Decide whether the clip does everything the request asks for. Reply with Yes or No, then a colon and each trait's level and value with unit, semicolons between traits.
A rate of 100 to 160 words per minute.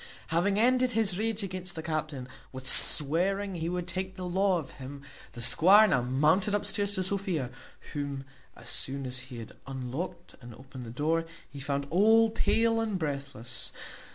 No: average, 170 wpm